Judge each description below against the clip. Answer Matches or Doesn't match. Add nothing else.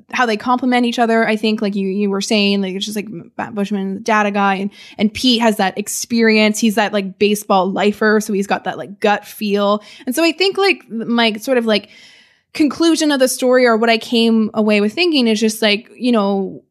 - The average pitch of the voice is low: Doesn't match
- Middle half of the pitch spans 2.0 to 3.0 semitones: Matches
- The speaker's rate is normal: Doesn't match